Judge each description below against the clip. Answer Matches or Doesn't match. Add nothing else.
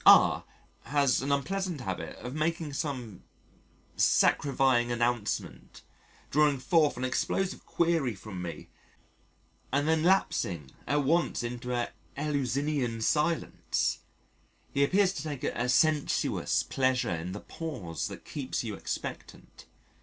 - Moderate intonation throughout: Matches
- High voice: Doesn't match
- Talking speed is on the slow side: Matches